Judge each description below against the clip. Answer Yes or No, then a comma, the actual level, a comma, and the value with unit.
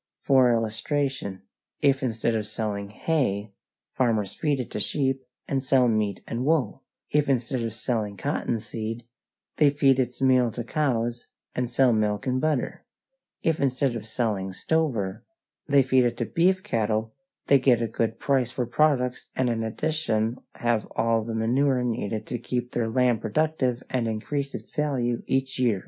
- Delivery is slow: No, average, 165 wpm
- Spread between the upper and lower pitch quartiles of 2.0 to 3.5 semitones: Yes, average, 3.2 semitones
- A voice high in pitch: No, low, 120 Hz